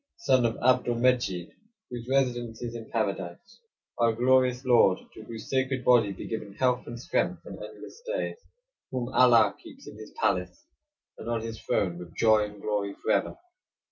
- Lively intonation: No, average, 3.3 semitones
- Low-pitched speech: Yes, low, 115 Hz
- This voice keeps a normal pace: Yes, average, 170 wpm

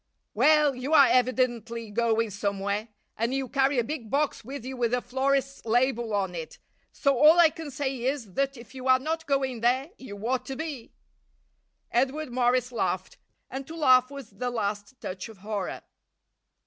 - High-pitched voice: Yes, very high, 255 Hz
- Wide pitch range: No, average, 3.2 semitones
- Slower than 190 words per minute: Yes, average, 175 wpm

